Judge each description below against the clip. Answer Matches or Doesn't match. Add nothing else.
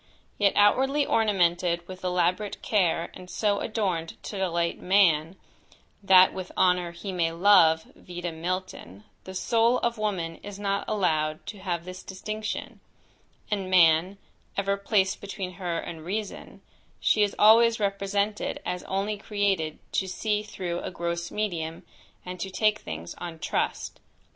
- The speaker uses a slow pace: Doesn't match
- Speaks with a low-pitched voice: Doesn't match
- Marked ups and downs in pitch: Doesn't match